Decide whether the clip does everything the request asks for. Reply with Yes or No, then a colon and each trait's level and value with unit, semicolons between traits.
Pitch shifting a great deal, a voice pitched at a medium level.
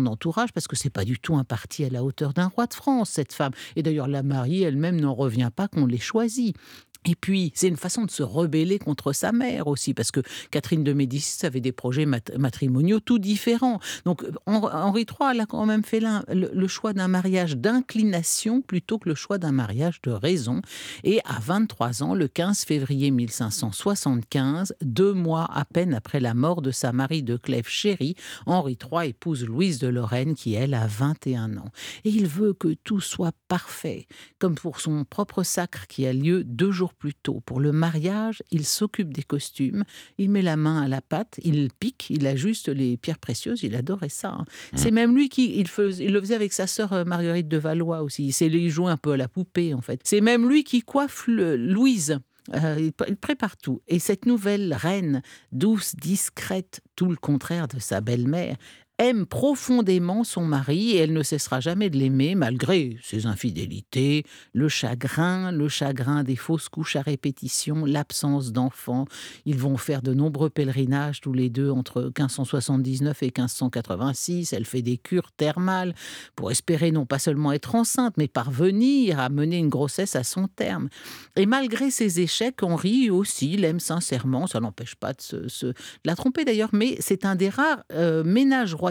Yes: wide, 6.2 semitones; medium, 160 Hz